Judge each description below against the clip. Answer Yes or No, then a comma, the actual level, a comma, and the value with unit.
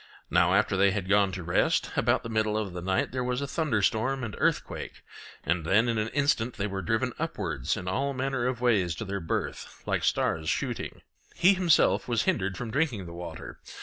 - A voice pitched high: No, low, 110 Hz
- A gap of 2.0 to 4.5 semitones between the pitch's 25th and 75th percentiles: No, average, 5.2 semitones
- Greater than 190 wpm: Yes, fast, 205 wpm